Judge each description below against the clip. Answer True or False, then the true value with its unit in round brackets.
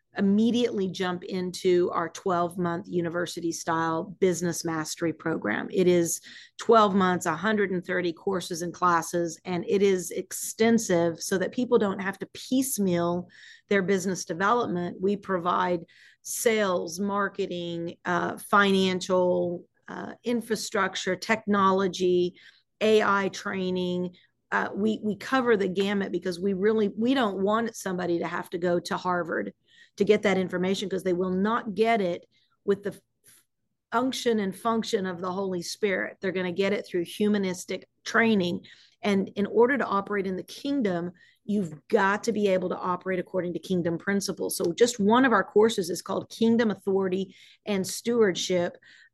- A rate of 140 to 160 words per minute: True (145 wpm)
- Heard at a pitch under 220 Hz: True (190 Hz)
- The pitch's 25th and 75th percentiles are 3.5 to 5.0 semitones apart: False (2.8 semitones)